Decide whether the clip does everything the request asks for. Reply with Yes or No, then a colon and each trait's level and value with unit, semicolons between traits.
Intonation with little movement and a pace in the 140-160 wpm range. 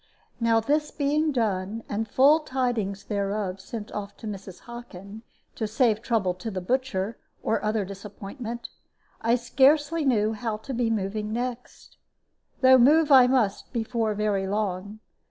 No: average, 3.7 semitones; average, 145 wpm